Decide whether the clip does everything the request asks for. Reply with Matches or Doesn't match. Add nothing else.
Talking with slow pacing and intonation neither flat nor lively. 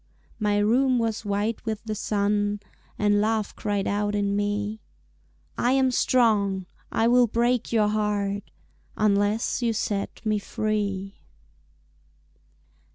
Doesn't match